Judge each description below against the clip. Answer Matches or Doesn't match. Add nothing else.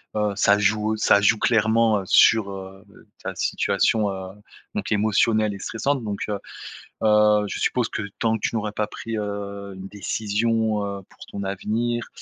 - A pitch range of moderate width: Doesn't match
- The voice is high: Doesn't match